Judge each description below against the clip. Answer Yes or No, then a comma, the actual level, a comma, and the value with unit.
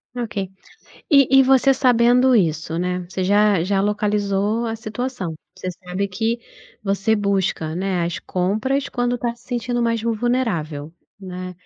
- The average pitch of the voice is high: Yes, high, 210 Hz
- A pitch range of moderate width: Yes, average, 4.7 semitones